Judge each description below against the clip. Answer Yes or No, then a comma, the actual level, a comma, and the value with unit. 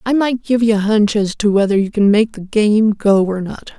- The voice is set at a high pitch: Yes, high, 210 Hz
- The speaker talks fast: Yes, fast, 270 wpm